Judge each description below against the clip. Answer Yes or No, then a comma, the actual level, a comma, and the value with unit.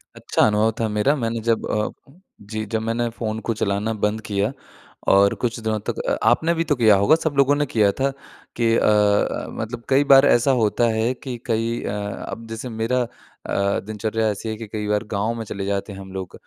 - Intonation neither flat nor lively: No, narrow, 2.2 semitones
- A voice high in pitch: No, low, 110 Hz